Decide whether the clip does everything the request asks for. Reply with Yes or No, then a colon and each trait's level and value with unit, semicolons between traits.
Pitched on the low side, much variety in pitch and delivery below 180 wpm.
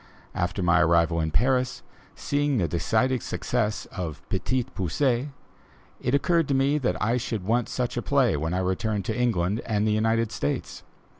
Yes: low, 110 Hz; wide, 5.9 semitones; average, 170 wpm